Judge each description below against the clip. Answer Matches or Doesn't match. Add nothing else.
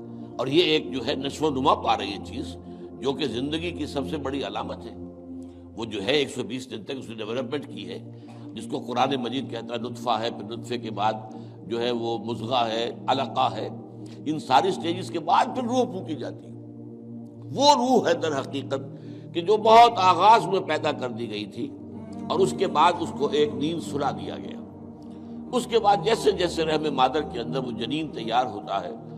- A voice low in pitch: Matches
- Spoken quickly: Matches